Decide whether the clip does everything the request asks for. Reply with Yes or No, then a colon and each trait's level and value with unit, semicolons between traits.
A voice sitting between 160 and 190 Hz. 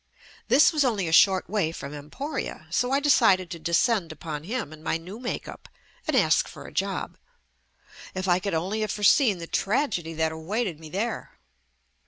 Yes: medium, 185 Hz